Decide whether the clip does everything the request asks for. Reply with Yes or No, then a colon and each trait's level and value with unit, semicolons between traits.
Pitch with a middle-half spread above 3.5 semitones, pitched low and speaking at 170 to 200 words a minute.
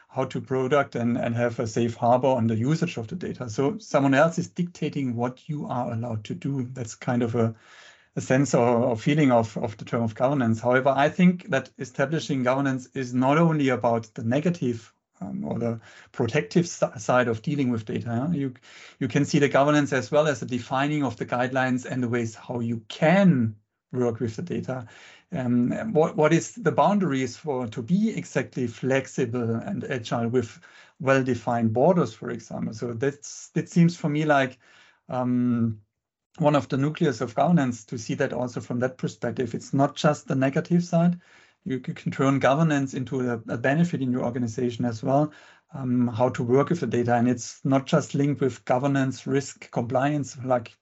No: average, 3.2 semitones; low, 130 Hz; average, 195 wpm